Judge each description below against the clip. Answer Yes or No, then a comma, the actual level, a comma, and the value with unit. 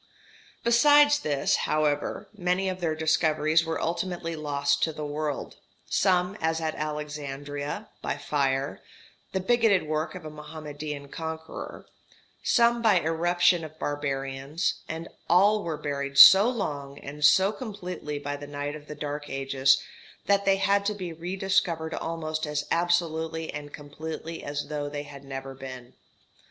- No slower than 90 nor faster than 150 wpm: Yes, average, 145 wpm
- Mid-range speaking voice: Yes, medium, 155 Hz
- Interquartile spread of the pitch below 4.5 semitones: Yes, average, 3.4 semitones